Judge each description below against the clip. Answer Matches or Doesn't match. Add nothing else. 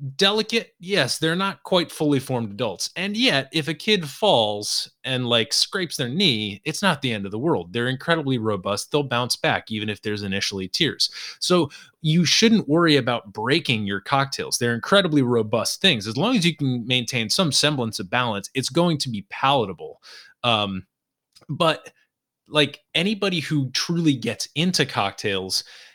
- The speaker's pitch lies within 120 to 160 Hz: Matches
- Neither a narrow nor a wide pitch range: Doesn't match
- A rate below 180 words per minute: Matches